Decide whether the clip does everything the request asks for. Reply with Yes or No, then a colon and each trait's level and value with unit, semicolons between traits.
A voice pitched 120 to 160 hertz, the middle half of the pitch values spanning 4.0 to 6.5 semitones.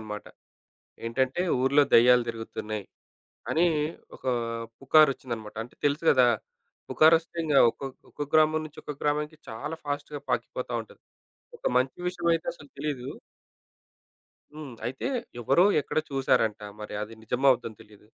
Yes: low, 135 Hz; average, 4.6 semitones